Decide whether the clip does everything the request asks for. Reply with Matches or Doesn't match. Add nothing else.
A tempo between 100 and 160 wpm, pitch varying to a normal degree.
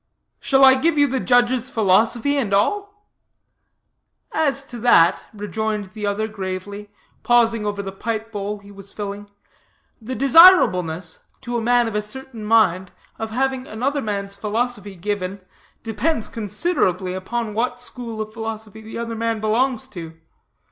Matches